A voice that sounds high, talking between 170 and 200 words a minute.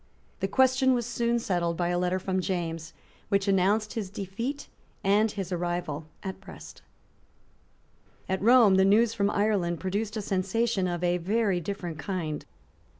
No: high, 195 Hz; average, 150 wpm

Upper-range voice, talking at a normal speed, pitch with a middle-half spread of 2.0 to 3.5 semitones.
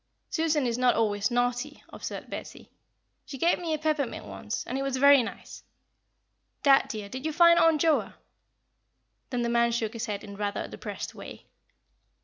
No: very high, 255 Hz; average, 175 wpm; average, 4.7 semitones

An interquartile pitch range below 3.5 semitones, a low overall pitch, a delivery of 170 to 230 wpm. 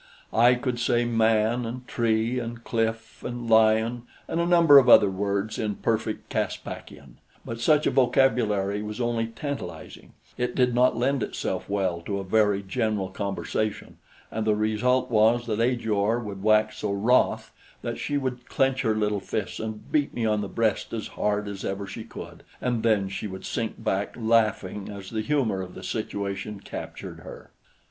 Yes: average, 2.8 semitones; low, 110 Hz; average, 175 wpm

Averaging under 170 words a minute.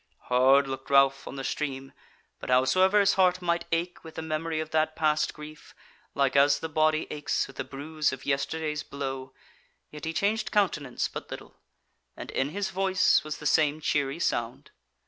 No: average, 180 wpm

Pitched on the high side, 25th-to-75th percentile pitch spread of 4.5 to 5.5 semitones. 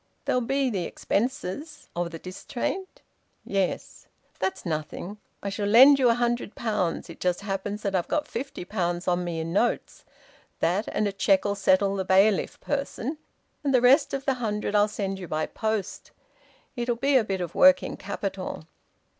Yes: high, 205 Hz; average, 4.9 semitones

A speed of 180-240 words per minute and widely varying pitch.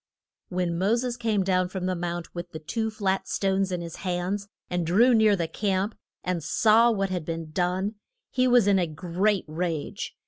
No: average, 195 wpm; average, 3.2 semitones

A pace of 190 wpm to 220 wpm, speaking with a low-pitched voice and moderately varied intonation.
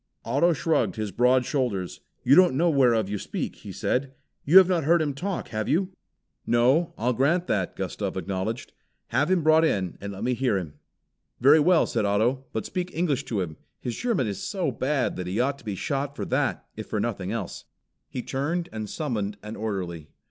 No: average, 200 wpm; low, 130 Hz; wide, 6.8 semitones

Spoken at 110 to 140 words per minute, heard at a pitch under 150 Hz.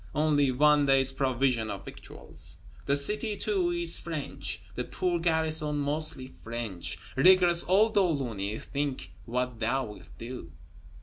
Yes: slow, 135 wpm; medium, 140 Hz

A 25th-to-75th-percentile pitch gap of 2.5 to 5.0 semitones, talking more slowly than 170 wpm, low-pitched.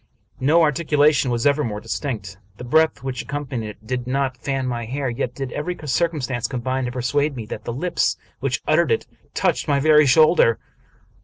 No: average, 3.4 semitones; average, 180 wpm; low, 130 Hz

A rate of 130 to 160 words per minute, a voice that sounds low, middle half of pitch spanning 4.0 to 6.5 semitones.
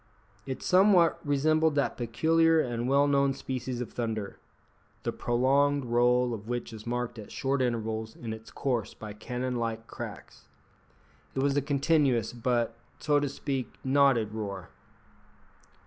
No: average, 145 wpm; low, 125 Hz; average, 3.5 semitones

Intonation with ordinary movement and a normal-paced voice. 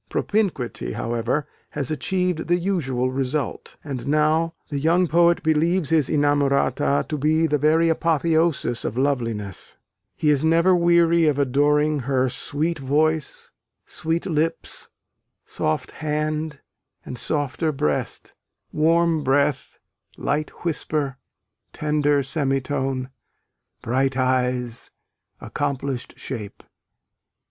No: average, 3.3 semitones; slow, 105 wpm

